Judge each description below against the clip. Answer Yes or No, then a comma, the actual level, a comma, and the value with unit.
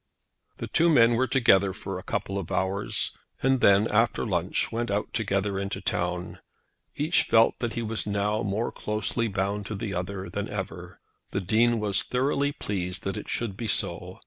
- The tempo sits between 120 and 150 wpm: No, average, 185 wpm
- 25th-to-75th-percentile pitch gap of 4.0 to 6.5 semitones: No, average, 3.1 semitones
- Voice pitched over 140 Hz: No, low, 105 Hz